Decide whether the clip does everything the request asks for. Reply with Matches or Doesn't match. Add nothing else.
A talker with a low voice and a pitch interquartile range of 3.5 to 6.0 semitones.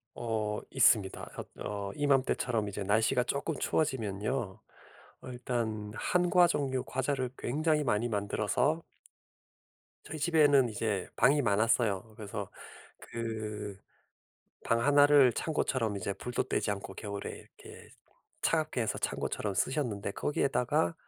Matches